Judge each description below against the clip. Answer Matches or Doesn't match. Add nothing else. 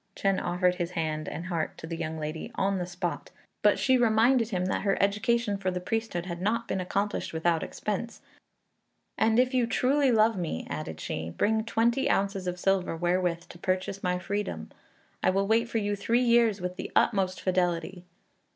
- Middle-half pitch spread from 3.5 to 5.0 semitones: Matches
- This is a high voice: Matches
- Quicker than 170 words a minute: Matches